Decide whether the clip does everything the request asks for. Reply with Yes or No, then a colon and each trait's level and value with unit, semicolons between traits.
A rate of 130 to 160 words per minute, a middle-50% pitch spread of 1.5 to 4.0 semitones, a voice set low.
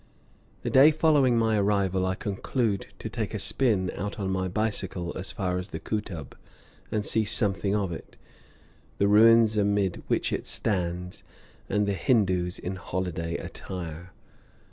Yes: average, 150 wpm; average, 3.0 semitones; low, 100 Hz